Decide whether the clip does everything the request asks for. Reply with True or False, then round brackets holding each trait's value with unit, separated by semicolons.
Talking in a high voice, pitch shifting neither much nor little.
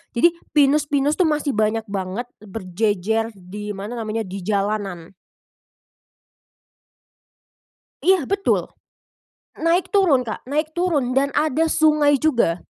False (245 Hz; 6.7 semitones)